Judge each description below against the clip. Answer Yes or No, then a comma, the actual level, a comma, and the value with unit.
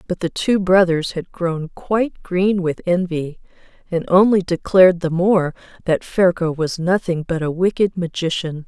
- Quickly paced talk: No, average, 160 wpm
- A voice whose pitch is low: No, medium, 175 Hz